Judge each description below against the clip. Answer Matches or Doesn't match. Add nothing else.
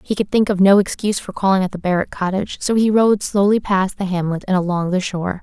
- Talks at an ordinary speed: Doesn't match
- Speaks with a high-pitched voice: Matches